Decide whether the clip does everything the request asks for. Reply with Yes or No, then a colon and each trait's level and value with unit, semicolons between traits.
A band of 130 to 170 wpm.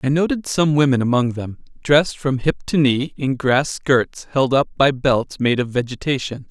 No: average, 195 wpm